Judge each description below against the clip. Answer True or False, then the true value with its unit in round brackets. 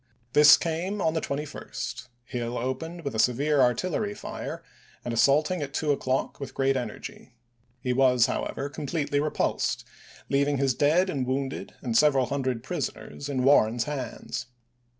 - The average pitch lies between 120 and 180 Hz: True (140 Hz)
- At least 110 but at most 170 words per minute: True (155 wpm)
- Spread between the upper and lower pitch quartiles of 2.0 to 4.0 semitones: True (2.9 semitones)